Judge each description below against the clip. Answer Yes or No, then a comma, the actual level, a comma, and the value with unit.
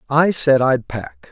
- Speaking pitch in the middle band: No, low, 130 Hz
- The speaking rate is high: No, average, 180 wpm